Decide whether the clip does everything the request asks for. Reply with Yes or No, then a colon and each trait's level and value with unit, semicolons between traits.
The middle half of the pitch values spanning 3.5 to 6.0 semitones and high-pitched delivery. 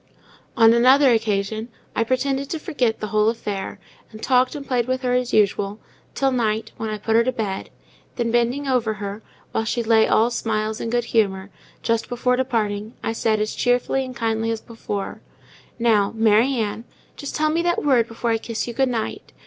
No: narrow, 2.6 semitones; high, 230 Hz